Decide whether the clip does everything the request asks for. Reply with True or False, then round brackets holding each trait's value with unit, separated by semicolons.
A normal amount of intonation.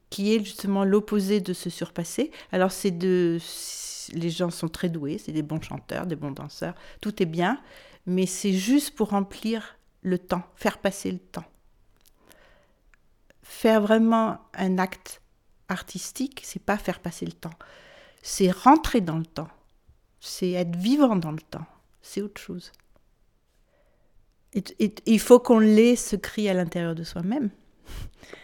True (3.8 semitones)